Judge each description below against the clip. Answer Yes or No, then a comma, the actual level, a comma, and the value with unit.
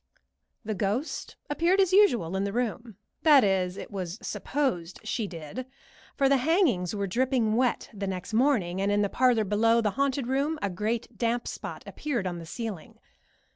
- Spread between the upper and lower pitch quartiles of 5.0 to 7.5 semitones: Yes, average, 5.3 semitones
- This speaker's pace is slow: No, average, 175 wpm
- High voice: Yes, high, 225 Hz